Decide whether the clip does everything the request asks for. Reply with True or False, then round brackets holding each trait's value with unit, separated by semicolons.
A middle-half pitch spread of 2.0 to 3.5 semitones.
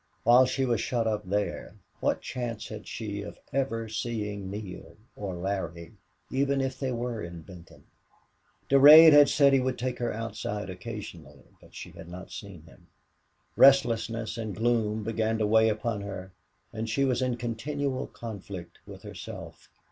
False (3.9 semitones)